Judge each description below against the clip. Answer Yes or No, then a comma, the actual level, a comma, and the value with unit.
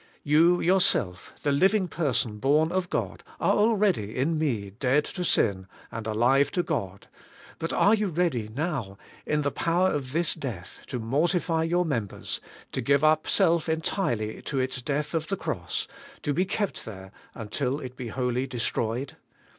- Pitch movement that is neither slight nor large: No, wide, 6.4 semitones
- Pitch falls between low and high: Yes, medium, 145 Hz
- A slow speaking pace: No, average, 165 wpm